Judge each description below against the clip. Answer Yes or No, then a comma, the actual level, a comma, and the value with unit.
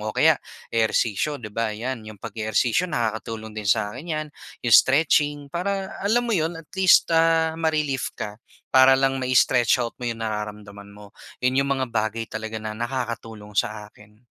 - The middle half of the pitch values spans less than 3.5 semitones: No, average, 5.2 semitones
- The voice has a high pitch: No, low, 115 Hz